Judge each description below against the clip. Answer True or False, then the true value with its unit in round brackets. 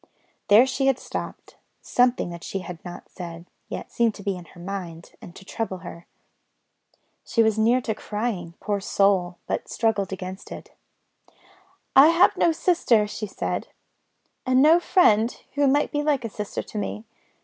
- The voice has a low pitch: False (210 Hz)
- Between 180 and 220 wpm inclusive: False (170 wpm)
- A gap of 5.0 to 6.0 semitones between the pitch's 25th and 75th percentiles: True (5.4 semitones)